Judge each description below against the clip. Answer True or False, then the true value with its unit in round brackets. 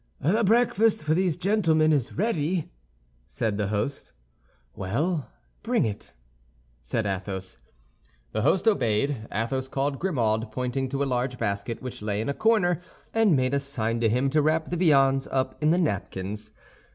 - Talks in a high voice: False (135 Hz)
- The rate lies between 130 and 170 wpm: True (160 wpm)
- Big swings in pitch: True (6.7 semitones)